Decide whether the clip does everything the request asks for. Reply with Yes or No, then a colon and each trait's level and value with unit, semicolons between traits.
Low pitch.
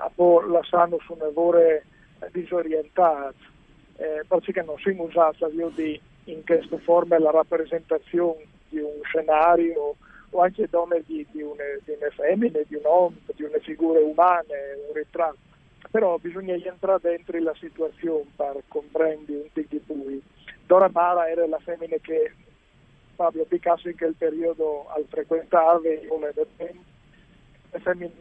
No: medium, 165 Hz